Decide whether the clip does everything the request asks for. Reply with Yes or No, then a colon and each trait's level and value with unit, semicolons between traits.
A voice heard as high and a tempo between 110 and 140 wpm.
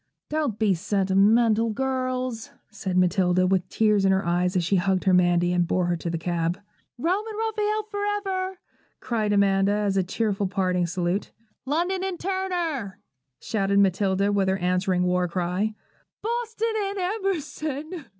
No: high, 205 Hz; average, 155 wpm